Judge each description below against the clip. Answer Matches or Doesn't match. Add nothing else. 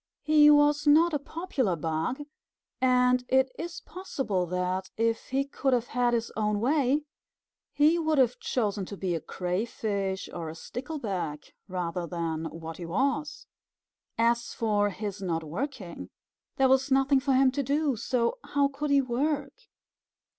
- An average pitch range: Doesn't match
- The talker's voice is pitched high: Matches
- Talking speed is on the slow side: Doesn't match